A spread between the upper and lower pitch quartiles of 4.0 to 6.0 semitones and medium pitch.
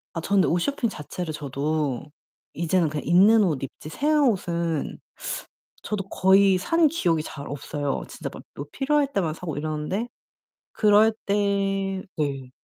Yes: average, 5.1 semitones; medium, 180 Hz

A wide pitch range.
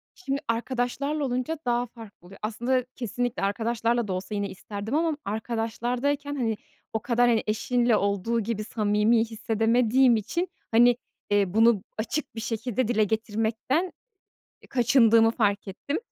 No: narrow, 2.4 semitones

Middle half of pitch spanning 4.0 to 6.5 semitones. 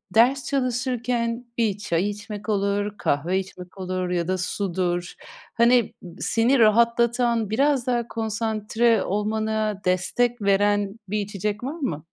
No: average, 3.2 semitones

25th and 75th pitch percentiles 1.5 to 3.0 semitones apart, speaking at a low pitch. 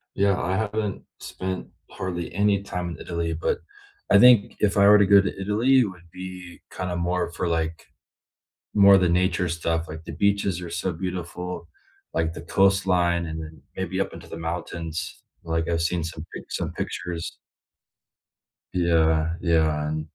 Yes: average, 2.7 semitones; very low, 90 Hz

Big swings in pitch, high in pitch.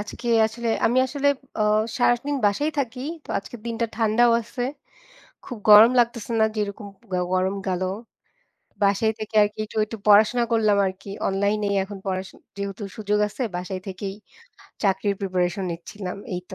No: average, 2.9 semitones; high, 210 Hz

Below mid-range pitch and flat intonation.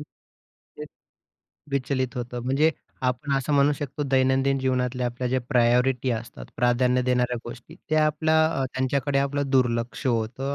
Yes: low, 130 Hz; narrow, 2.1 semitones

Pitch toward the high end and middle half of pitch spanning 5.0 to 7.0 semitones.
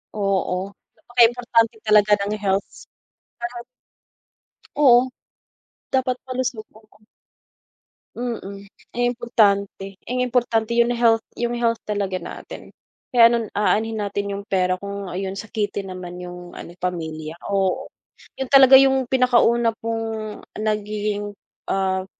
No: high, 215 Hz; average, 3.4 semitones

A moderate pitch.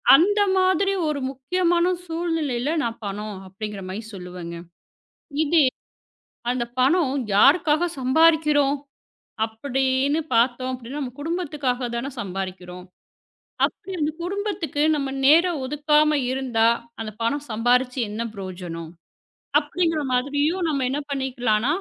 No: very high, 270 Hz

